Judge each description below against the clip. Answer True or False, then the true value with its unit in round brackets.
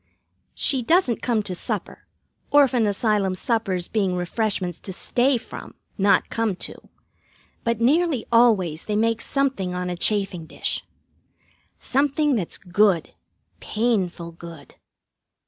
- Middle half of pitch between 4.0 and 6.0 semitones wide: True (5.0 semitones)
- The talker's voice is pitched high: True (215 Hz)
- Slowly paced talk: True (120 wpm)